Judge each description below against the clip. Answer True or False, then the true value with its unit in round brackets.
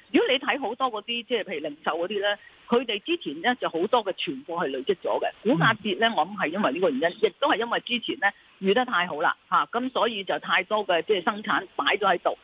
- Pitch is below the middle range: False (240 Hz)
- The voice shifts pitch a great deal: True (8.9 semitones)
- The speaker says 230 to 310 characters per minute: False (365 characters per minute)